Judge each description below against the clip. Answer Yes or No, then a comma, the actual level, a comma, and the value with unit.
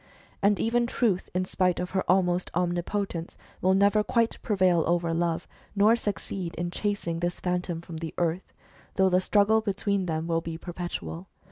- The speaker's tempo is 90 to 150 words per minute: No, average, 165 wpm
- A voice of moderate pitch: Yes, medium, 180 Hz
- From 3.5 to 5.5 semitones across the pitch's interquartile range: No, average, 2.8 semitones